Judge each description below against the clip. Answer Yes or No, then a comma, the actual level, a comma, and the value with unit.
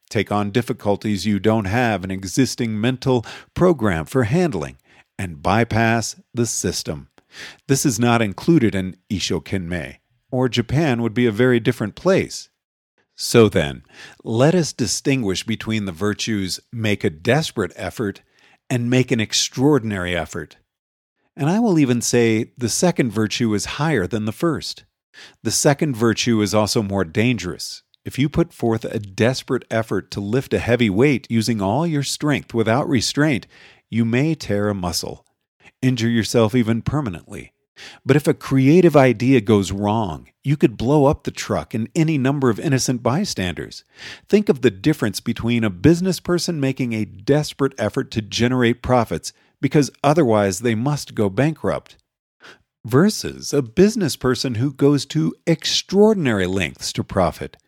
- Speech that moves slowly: No, average, 150 wpm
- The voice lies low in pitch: Yes, low, 120 Hz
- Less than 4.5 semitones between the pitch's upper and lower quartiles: No, average, 4.8 semitones